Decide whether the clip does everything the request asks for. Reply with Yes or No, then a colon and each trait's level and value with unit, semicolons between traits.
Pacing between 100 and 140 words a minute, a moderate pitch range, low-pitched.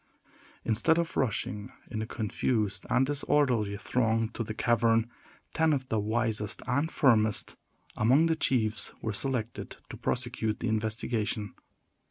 Yes: slow, 135 wpm; average, 3.0 semitones; low, 115 Hz